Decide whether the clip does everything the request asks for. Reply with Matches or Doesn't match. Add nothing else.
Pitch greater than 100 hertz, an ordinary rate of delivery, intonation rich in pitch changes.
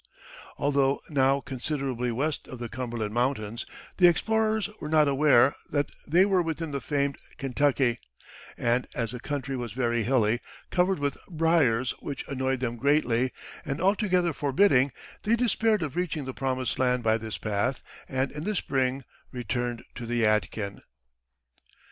Doesn't match